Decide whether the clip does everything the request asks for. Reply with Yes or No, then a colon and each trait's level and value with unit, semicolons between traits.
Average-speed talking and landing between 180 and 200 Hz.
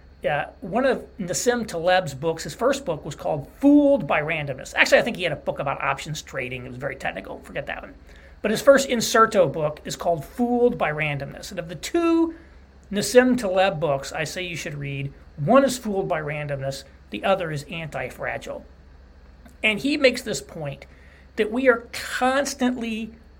Yes: average, 185 wpm; medium, 185 Hz